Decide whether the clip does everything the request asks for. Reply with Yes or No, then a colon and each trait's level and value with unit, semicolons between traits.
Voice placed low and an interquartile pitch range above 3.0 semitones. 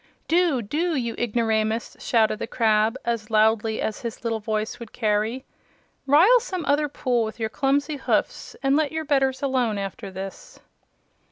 No: high, 235 Hz; average, 4.6 semitones